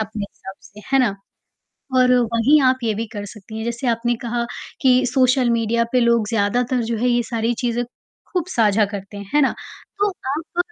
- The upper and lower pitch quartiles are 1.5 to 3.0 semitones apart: Yes, narrow, 2.5 semitones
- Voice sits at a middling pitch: No, high, 235 Hz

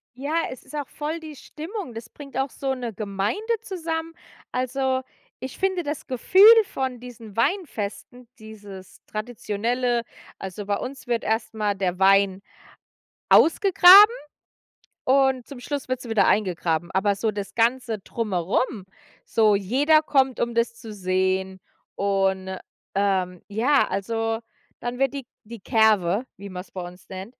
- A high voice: Yes, high, 230 Hz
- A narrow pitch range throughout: No, average, 5.3 semitones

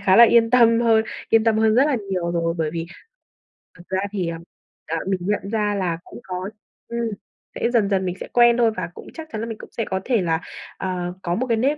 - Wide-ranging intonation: No, average, 4.3 semitones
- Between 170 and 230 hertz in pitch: Yes, high, 210 Hz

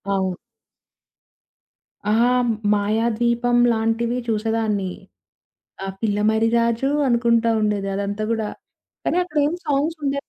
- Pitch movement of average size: No, narrow, 2.1 semitones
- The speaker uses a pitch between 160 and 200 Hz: No, high, 225 Hz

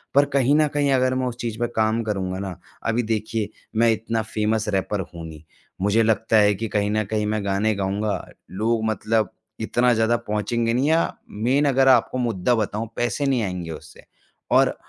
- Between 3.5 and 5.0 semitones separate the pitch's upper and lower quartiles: No, narrow, 2.5 semitones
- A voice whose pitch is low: Yes, low, 110 Hz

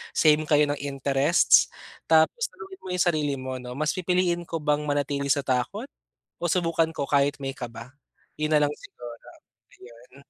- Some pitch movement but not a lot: Yes, average, 3.0 semitones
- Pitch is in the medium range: Yes, medium, 145 Hz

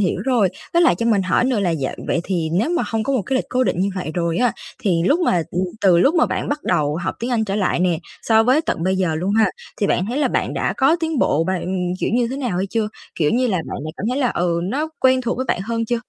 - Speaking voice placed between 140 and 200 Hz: No, high, 215 Hz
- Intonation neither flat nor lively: No, wide, 6.1 semitones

